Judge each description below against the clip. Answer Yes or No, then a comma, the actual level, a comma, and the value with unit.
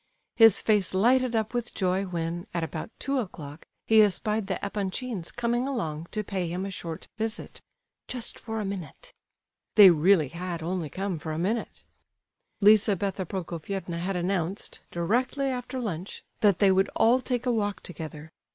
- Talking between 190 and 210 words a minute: No, average, 160 wpm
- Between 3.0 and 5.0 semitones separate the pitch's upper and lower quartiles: Yes, average, 4.4 semitones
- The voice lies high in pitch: Yes, high, 195 Hz